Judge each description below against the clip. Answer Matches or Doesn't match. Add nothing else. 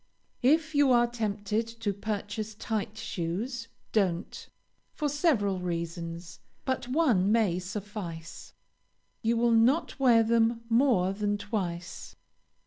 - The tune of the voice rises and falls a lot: Doesn't match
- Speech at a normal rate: Doesn't match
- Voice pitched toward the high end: Matches